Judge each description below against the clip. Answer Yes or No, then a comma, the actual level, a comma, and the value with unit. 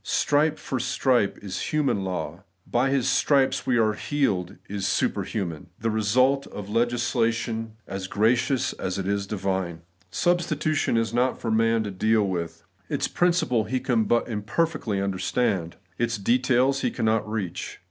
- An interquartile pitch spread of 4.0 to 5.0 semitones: Yes, average, 4.5 semitones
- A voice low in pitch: Yes, low, 115 Hz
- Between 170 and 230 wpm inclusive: No, average, 160 wpm